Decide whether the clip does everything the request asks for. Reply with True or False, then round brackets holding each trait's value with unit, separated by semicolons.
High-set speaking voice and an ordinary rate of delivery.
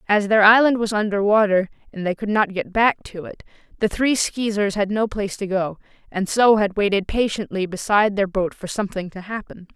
False (205 Hz; 210 wpm)